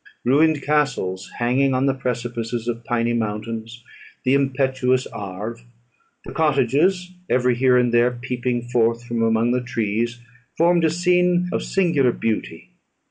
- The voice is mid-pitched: No, low, 125 Hz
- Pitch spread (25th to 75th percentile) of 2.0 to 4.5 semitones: Yes, average, 2.9 semitones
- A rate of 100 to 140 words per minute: Yes, slow, 135 wpm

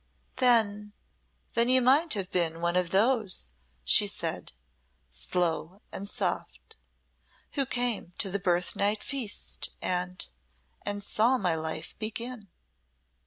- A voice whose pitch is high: Yes, high, 205 Hz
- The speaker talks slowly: Yes, slow, 120 wpm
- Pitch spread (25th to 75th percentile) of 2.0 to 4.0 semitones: No, average, 4.9 semitones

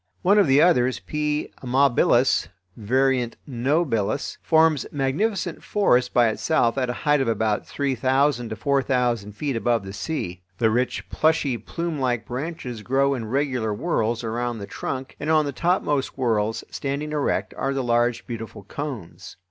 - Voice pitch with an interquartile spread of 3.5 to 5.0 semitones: Yes, average, 4.0 semitones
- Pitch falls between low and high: No, low, 130 Hz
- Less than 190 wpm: Yes, average, 155 wpm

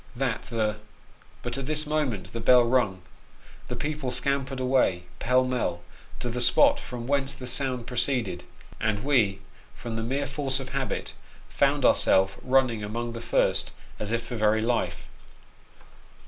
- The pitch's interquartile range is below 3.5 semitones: Yes, average, 3.1 semitones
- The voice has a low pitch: Yes, low, 125 Hz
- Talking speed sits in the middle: Yes, average, 160 wpm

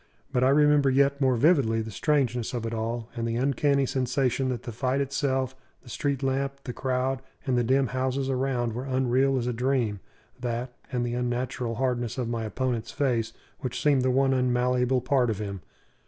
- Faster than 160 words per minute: Yes, average, 190 wpm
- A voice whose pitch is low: Yes, low, 125 Hz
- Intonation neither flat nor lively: No, narrow, 2.0 semitones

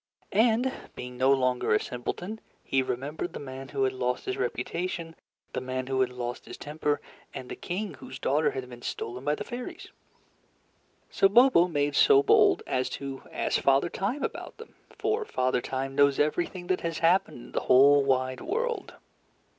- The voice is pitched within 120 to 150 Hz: Yes, medium, 140 Hz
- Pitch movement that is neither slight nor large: No, wide, 6.5 semitones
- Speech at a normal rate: Yes, average, 180 wpm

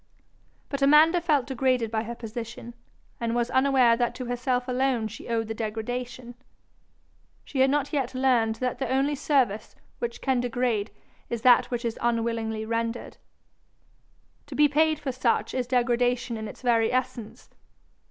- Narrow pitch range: Yes, narrow, 2.3 semitones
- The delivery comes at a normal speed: Yes, average, 155 wpm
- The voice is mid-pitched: No, high, 245 Hz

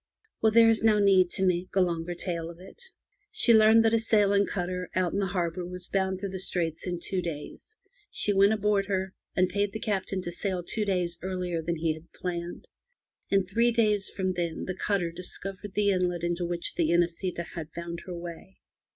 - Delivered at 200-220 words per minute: Yes, fast, 205 wpm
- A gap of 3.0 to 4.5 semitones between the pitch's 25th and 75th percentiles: No, narrow, 2.6 semitones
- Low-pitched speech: No, medium, 185 Hz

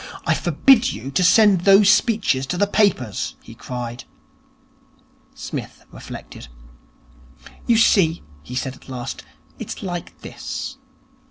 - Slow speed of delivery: Yes, slow, 125 wpm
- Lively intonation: Yes, wide, 8.0 semitones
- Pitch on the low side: No, medium, 175 Hz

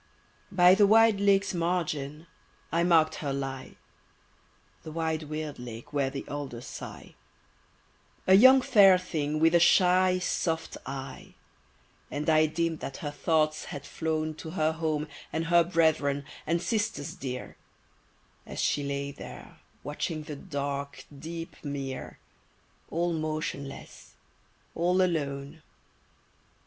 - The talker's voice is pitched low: No, medium, 155 Hz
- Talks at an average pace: No, slow, 125 wpm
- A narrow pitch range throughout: No, average, 3.3 semitones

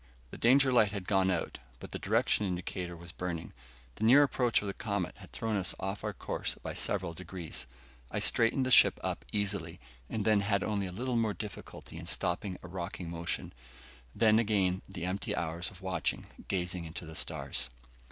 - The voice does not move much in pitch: No, average, 3.5 semitones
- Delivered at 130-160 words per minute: No, average, 185 wpm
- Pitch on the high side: No, very low, 95 Hz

